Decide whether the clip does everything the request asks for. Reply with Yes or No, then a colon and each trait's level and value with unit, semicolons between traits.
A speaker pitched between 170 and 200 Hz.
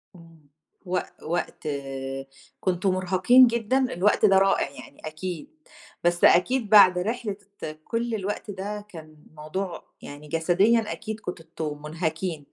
Yes: medium, 185 Hz